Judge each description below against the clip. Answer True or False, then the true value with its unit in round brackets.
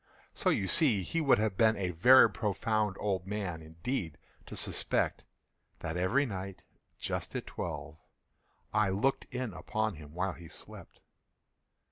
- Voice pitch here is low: True (100 Hz)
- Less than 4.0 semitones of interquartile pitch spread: True (3.6 semitones)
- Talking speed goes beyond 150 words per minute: False (145 wpm)